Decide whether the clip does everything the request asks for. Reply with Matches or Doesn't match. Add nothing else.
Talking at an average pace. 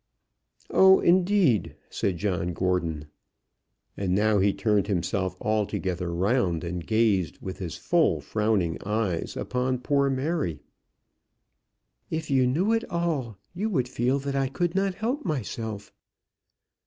Doesn't match